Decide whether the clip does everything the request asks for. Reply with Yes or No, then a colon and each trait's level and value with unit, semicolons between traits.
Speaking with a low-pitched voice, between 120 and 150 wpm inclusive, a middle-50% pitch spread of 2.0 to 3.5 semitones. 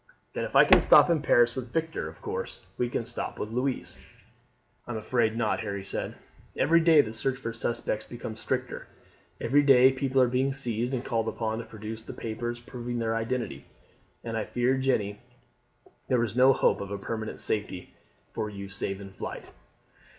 No: low, 120 Hz; average, 185 wpm; average, 2.9 semitones